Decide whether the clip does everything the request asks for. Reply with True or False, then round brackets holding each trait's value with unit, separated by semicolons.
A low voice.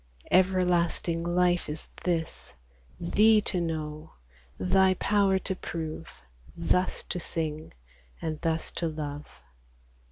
False (170 Hz)